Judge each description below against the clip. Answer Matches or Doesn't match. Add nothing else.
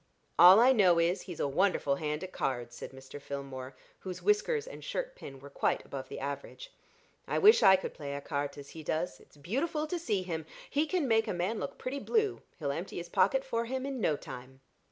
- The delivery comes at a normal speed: Doesn't match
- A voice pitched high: Doesn't match